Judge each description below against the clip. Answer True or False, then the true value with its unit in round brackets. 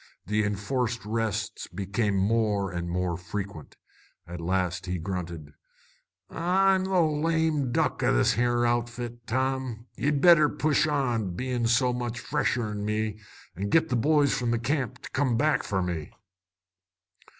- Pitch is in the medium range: False (115 Hz)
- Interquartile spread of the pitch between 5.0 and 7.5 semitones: True (5.3 semitones)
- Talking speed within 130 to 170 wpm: True (145 wpm)